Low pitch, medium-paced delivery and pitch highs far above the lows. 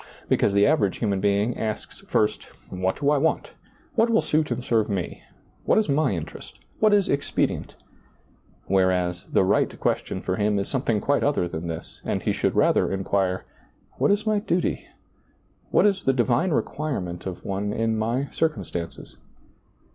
Yes: low, 110 Hz; average, 180 wpm; wide, 7.5 semitones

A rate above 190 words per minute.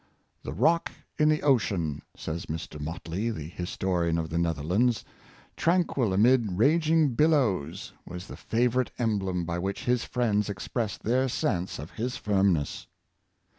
No: average, 150 wpm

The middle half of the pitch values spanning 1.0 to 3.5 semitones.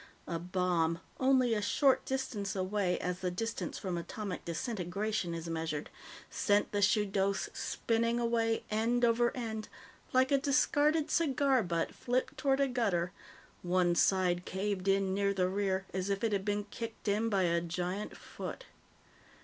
No: average, 4.3 semitones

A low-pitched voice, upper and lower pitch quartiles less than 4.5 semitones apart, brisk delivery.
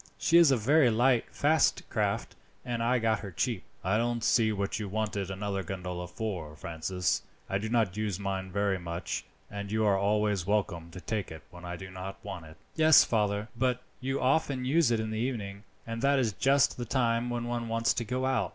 Yes: low, 110 Hz; average, 3.9 semitones; fast, 210 wpm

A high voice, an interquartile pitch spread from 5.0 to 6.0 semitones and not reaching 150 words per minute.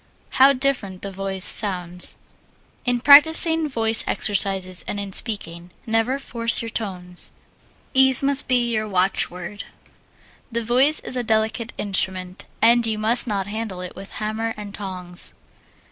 No: high, 215 Hz; average, 4.0 semitones; average, 140 wpm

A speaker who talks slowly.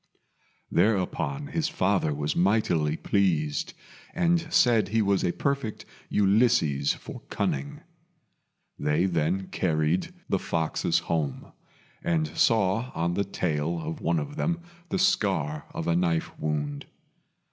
Yes: slow, 125 wpm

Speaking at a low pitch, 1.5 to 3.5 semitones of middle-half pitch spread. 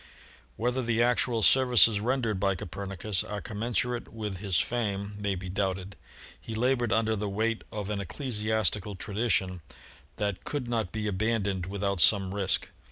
Yes: low, 105 Hz; average, 2.8 semitones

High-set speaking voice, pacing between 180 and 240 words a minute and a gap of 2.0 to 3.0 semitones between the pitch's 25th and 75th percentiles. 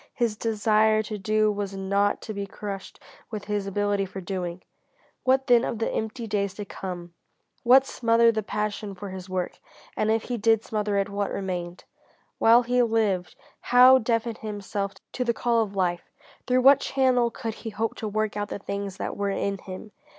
Yes: high, 210 Hz; average, 185 wpm; narrow, 2.4 semitones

